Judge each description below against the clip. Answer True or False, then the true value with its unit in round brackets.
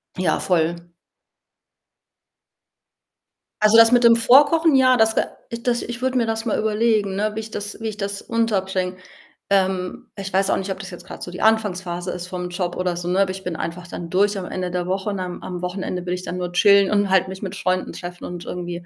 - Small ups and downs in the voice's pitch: False (3.2 semitones)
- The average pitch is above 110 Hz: True (190 Hz)